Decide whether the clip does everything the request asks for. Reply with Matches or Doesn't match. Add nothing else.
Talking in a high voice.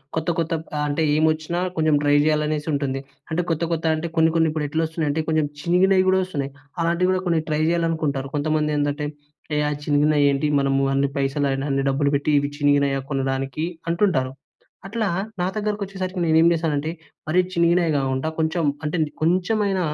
Doesn't match